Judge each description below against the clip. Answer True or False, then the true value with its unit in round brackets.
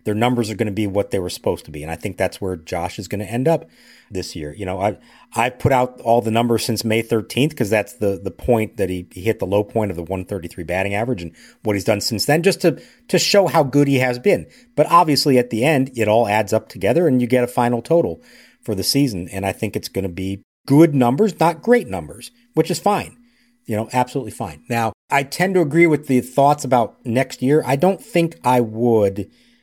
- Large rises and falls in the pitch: True (5.9 semitones)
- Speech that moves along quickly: True (250 wpm)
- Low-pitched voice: True (120 Hz)